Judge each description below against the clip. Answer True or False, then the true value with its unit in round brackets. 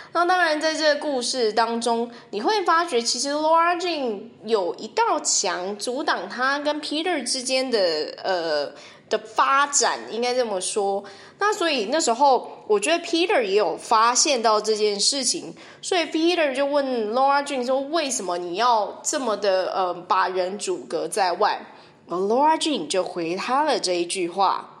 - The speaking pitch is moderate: False (265 Hz)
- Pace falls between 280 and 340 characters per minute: True (300 characters per minute)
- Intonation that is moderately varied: False (7.3 semitones)